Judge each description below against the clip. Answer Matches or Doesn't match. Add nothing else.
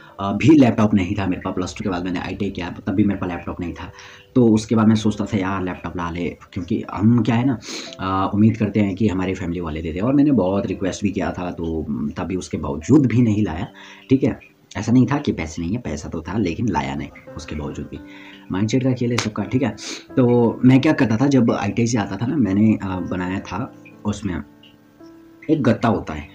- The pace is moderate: Doesn't match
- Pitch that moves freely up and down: Doesn't match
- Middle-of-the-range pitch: Doesn't match